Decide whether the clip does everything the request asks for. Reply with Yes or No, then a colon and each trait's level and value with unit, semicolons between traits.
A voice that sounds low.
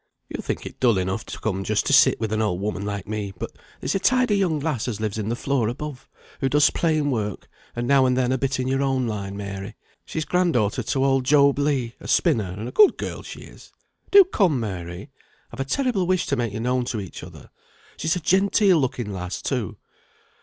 Yes: low, 125 Hz